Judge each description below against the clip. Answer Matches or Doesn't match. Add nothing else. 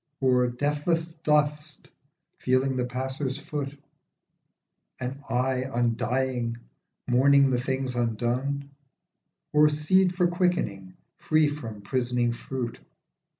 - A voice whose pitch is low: Matches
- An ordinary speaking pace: Doesn't match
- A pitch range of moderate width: Matches